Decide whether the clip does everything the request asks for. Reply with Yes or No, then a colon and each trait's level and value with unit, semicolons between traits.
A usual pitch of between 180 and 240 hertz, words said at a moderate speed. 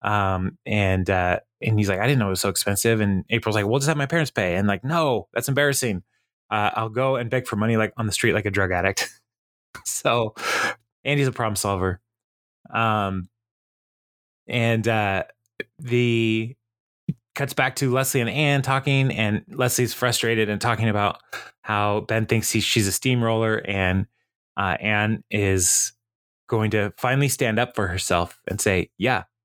No: low, 110 Hz; average, 175 wpm